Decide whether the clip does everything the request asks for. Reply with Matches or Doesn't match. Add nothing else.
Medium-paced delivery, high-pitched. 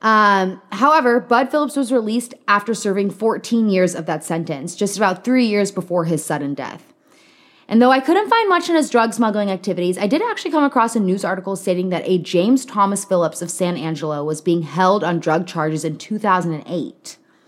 Matches